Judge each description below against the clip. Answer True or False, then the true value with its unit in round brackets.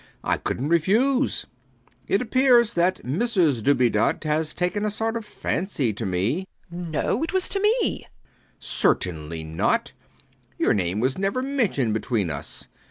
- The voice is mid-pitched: True (170 Hz)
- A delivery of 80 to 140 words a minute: False (160 wpm)